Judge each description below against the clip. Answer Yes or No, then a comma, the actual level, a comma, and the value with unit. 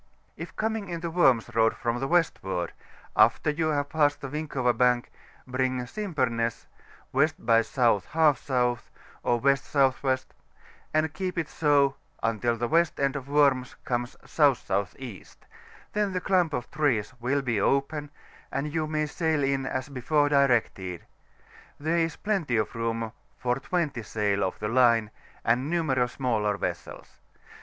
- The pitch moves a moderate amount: Yes, average, 4.4 semitones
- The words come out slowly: No, average, 145 wpm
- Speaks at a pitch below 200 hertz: Yes, low, 135 Hz